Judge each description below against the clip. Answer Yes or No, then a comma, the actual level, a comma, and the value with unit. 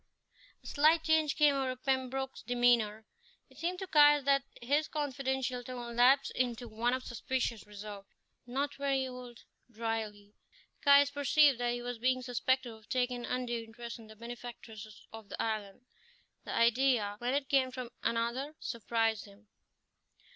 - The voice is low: No, high, 245 Hz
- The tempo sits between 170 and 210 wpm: No, average, 155 wpm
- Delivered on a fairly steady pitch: No, average, 3.0 semitones